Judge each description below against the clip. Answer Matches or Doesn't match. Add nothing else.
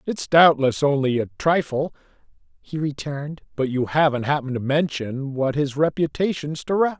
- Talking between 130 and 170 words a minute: Matches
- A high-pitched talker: Doesn't match